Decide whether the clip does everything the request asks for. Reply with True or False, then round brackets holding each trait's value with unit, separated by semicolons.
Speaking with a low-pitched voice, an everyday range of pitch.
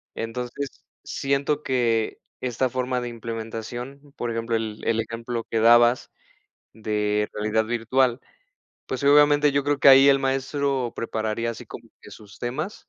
True (120 Hz; 3.1 semitones)